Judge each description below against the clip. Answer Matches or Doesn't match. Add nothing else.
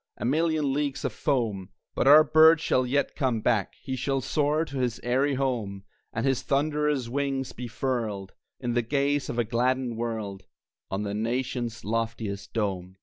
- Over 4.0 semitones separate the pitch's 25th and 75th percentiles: Doesn't match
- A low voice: Matches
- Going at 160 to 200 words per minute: Matches